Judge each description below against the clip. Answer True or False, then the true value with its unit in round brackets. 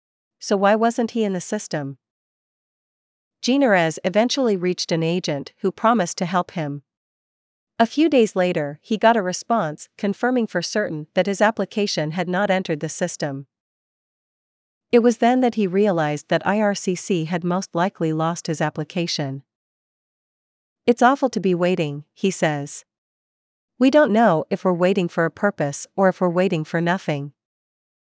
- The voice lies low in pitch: False (180 Hz)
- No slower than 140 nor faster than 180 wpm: True (155 wpm)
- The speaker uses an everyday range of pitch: True (4.9 semitones)